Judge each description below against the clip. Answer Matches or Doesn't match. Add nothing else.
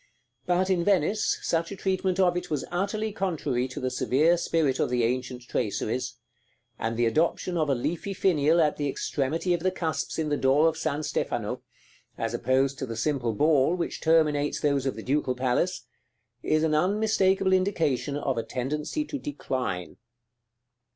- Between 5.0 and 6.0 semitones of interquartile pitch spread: Matches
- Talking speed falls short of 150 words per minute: Doesn't match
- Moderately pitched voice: Matches